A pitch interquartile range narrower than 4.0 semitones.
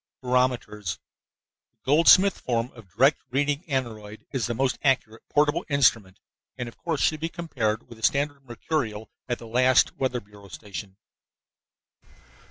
No: average, 4.3 semitones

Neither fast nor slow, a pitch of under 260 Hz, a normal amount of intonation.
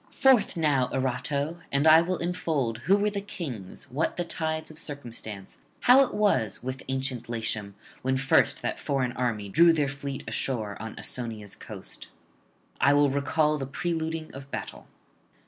Yes: average, 160 wpm; medium, 140 Hz; average, 4.8 semitones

